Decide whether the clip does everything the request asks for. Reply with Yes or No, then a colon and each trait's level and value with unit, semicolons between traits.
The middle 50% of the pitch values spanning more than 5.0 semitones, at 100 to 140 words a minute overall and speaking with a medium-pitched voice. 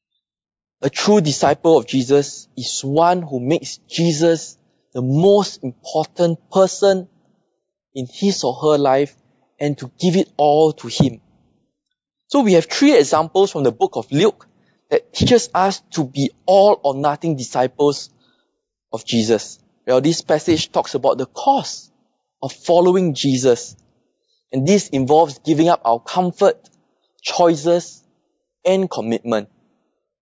Yes: wide, 5.5 semitones; slow, 135 wpm; medium, 165 Hz